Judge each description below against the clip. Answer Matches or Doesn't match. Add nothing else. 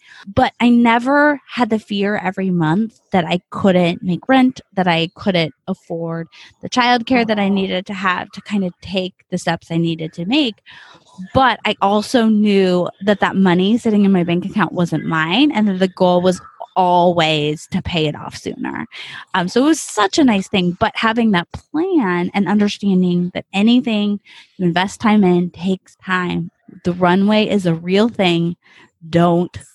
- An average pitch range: Matches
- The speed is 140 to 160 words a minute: Doesn't match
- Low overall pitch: Doesn't match